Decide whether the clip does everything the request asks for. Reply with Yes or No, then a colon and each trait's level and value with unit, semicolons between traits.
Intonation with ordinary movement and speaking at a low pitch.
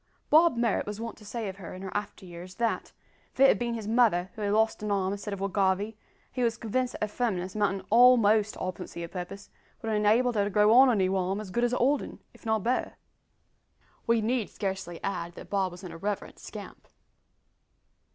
No: average, 3.3 semitones; high, 210 Hz